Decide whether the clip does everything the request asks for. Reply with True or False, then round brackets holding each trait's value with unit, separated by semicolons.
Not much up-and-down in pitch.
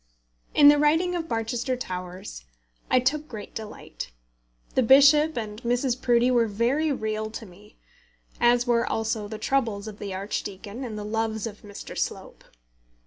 False (3.6 semitones)